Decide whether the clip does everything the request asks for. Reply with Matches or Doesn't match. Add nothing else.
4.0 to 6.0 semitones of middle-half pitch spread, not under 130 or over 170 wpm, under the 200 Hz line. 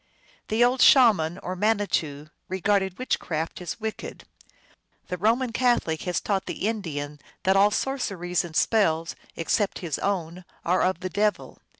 Matches